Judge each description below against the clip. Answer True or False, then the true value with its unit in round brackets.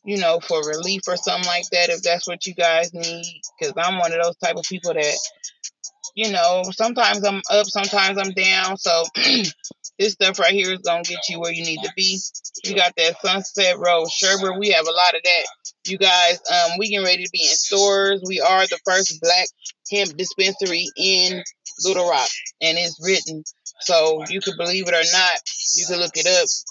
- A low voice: False (185 Hz)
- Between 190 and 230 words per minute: True (205 wpm)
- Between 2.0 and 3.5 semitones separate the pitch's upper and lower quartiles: True (2.6 semitones)